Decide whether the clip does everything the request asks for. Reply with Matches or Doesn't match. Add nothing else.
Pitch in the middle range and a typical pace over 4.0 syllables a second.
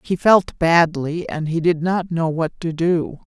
Doesn't match